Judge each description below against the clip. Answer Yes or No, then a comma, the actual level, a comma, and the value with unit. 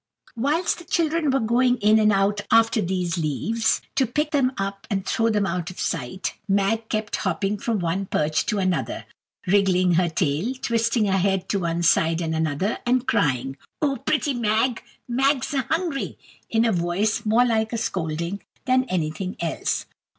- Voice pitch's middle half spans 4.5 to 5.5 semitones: Yes, average, 5.1 semitones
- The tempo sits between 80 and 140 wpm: No, average, 170 wpm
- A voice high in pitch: Yes, high, 210 Hz